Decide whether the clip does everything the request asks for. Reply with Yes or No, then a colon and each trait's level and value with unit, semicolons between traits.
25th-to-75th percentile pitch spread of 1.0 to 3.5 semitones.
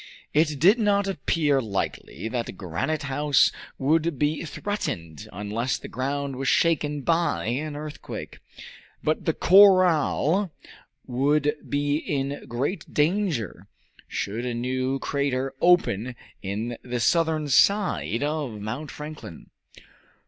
No: average, 4.4 semitones